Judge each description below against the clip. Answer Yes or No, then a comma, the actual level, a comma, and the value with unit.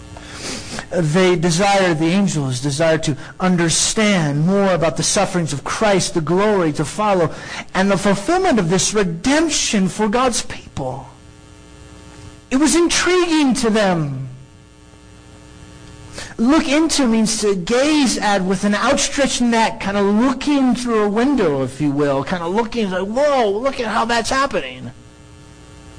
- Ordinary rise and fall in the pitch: No, wide, 6.2 semitones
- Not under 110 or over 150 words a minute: Yes, average, 140 wpm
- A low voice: No, high, 200 Hz